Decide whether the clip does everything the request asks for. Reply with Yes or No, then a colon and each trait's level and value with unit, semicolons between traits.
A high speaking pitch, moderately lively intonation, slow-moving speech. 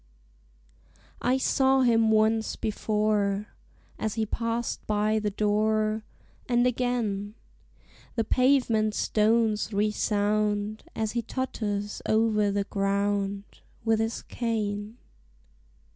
No: high, 215 Hz; narrow, 1.7 semitones; slow, 100 wpm